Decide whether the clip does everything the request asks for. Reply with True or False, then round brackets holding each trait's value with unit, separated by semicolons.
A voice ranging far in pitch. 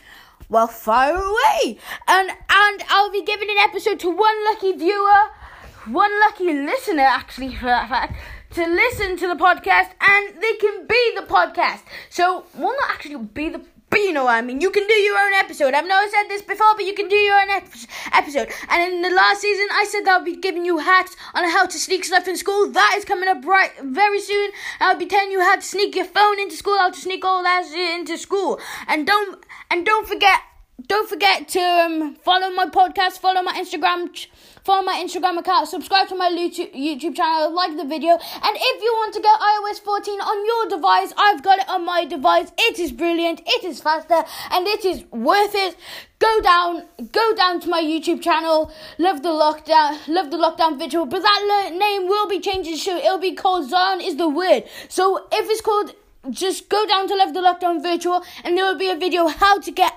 False (3.0 semitones)